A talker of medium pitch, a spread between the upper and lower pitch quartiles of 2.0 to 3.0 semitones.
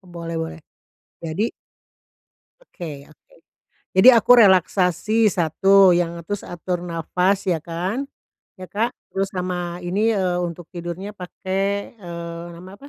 Yes: medium, 180 Hz; average, 2.7 semitones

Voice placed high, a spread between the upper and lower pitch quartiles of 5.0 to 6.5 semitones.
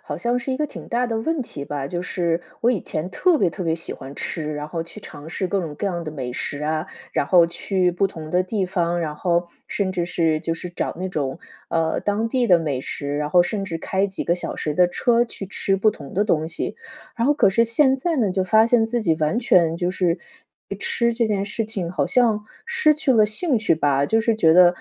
No: medium, 180 Hz; wide, 5.4 semitones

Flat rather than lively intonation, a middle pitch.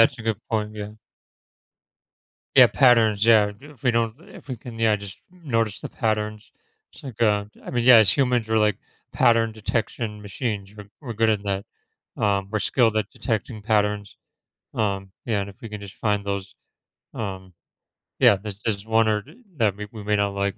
No: narrow, 2.0 semitones; low, 105 Hz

